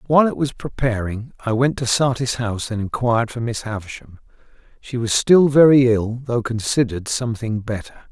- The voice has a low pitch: Yes, low, 120 Hz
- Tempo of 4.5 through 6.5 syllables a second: Yes, 5.5 syllables/s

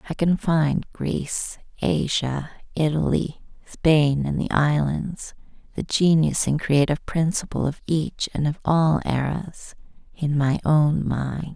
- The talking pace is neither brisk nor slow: No, slow, 125 wpm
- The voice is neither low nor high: Yes, medium, 150 Hz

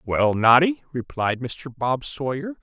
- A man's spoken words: Yes, male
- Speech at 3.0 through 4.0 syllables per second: Yes, 3.8 syllables/s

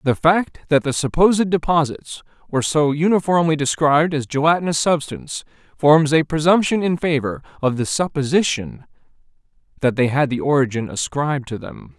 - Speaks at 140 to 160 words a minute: Yes, average, 145 wpm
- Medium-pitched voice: Yes, medium, 150 Hz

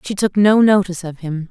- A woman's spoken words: Yes, female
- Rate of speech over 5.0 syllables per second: Yes, 5.7 syllables/s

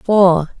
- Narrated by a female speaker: Yes, female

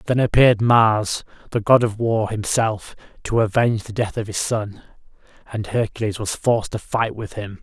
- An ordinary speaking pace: Yes, average, 180 wpm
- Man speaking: Yes, male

